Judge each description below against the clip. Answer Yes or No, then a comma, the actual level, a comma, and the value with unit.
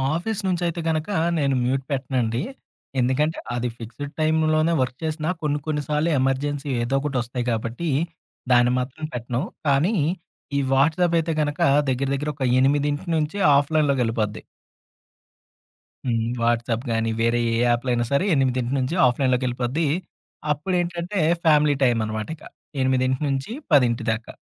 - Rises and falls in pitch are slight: No, average, 4.0 semitones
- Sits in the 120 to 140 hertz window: Yes, low, 135 Hz